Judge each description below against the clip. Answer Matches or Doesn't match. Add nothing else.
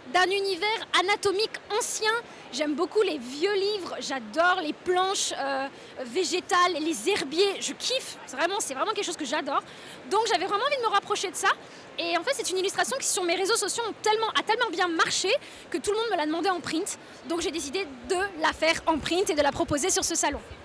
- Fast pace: Matches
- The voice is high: Matches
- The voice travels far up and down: Doesn't match